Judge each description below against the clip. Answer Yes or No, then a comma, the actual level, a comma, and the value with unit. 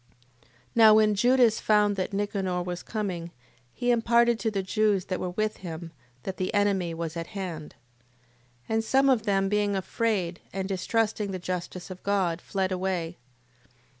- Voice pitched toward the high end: Yes, high, 195 Hz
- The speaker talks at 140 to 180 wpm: Yes, average, 165 wpm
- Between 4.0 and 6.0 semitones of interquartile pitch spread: No, average, 3.0 semitones